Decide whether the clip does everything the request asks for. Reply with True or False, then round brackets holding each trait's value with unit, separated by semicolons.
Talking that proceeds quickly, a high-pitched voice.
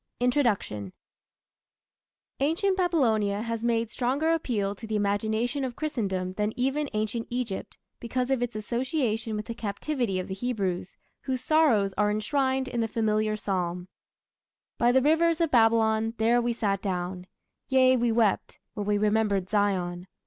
False (150 wpm; 225 Hz)